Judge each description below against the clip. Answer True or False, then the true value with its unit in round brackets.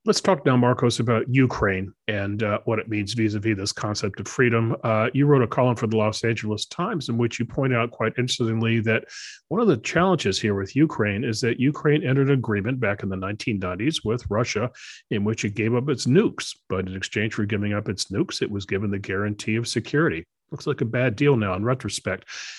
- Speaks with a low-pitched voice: True (115 Hz)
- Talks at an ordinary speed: False (225 wpm)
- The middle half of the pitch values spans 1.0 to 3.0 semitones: False (3.4 semitones)